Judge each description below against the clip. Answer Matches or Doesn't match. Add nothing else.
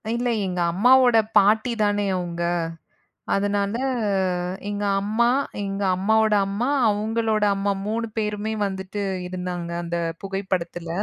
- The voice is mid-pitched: Doesn't match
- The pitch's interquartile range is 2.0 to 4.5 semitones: Matches